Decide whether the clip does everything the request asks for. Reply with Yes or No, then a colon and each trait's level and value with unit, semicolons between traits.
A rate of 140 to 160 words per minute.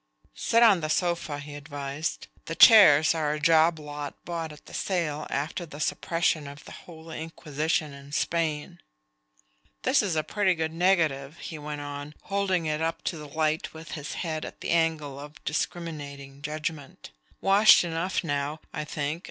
No: average, 170 wpm